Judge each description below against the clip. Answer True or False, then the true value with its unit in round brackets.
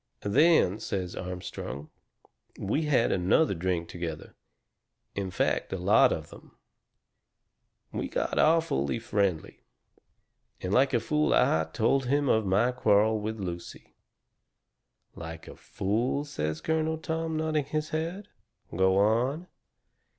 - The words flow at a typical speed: False (120 wpm)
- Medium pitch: False (110 Hz)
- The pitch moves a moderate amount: False (8.5 semitones)